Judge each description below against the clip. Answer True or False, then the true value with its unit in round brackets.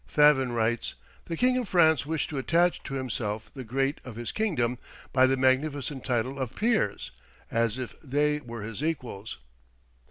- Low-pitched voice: True (130 Hz)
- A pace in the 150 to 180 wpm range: True (165 wpm)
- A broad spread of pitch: False (4.2 semitones)